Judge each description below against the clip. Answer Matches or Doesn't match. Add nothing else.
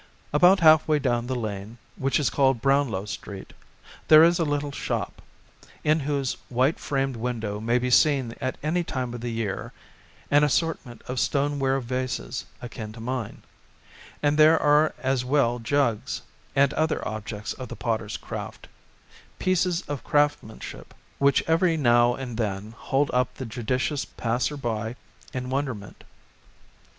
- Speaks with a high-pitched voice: Doesn't match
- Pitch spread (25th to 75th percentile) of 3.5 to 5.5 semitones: Matches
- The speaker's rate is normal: Matches